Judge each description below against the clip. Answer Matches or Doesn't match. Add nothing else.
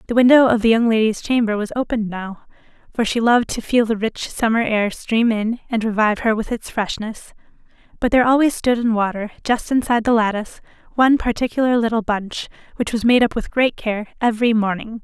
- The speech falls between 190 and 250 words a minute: Matches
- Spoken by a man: Doesn't match